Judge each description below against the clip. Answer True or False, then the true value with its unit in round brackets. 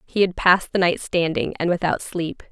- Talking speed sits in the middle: False (215 wpm)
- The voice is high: False (175 Hz)